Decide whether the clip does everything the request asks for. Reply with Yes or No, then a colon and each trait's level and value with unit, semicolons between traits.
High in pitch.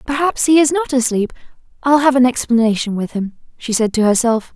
Yes: very high, 250 Hz